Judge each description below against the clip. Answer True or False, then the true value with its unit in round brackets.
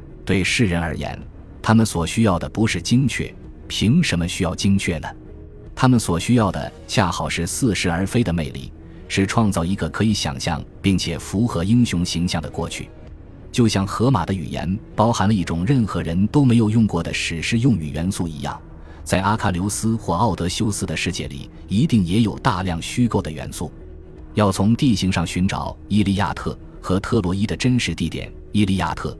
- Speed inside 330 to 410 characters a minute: False (280 characters per minute)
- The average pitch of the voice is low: True (95 Hz)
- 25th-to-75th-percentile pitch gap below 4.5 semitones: False (4.8 semitones)